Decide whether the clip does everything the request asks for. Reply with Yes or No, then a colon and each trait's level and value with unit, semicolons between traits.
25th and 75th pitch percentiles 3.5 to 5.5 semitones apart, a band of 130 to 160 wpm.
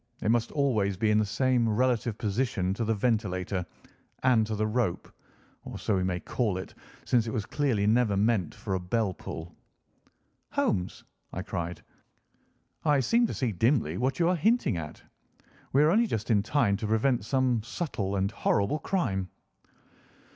No: average, 4.7 semitones; average, 170 wpm